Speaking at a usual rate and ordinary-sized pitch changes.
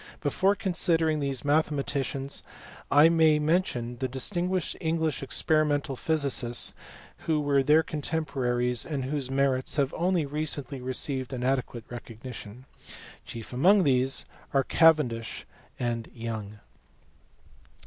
No: slow, 115 wpm; average, 3.9 semitones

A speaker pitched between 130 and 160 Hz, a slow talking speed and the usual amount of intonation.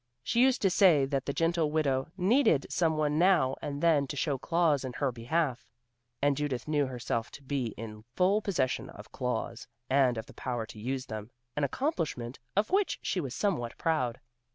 No: medium, 140 Hz; average, 190 wpm; average, 4.9 semitones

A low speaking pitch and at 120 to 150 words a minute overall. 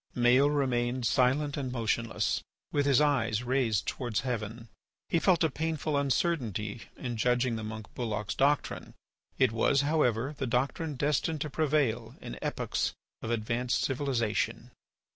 Yes: low, 125 Hz; average, 140 wpm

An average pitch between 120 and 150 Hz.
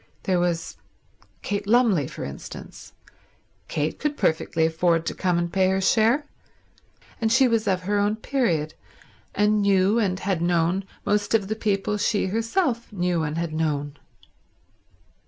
No: high, 190 Hz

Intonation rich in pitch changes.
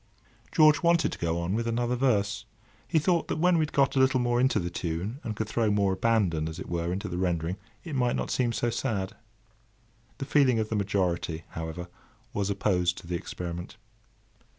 Yes: wide, 6.4 semitones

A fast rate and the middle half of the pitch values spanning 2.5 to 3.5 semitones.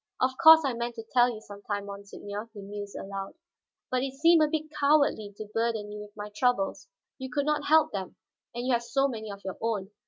No: fast, 225 wpm; average, 4.8 semitones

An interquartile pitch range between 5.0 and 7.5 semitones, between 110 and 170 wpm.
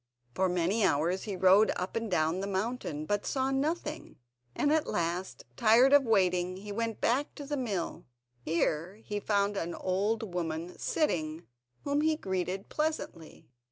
Yes: wide, 5.4 semitones; average, 160 wpm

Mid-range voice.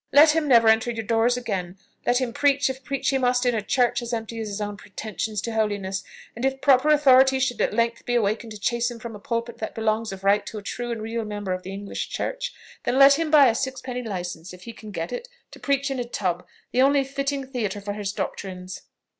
No: high, 230 Hz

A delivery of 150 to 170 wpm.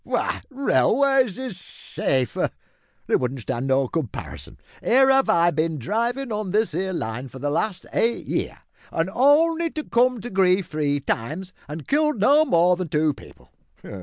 Yes: average, 165 wpm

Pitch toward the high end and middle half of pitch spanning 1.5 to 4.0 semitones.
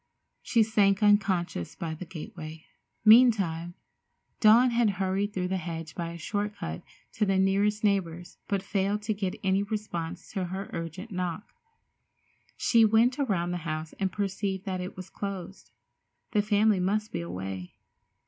Yes: high, 195 Hz; average, 3.3 semitones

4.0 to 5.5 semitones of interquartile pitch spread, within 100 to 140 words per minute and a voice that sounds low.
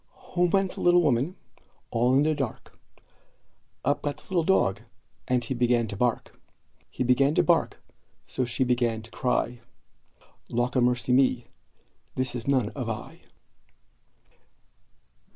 No: average, 3.0 semitones; slow, 135 wpm; low, 125 Hz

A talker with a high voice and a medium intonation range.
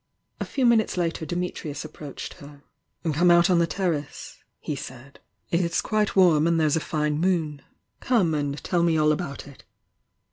No: medium, 165 Hz; average, 3.1 semitones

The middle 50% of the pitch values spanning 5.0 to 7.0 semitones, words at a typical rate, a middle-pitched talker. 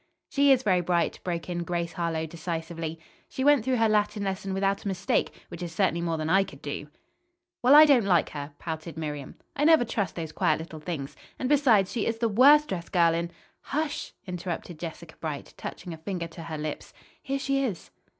No: wide, 5.5 semitones; fast, 210 wpm; medium, 175 Hz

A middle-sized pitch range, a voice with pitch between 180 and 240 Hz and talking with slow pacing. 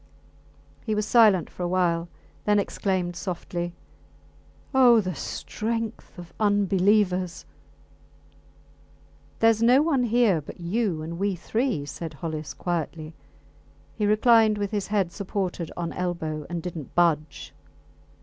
Yes: average, 4.0 semitones; medium, 185 Hz; slow, 125 wpm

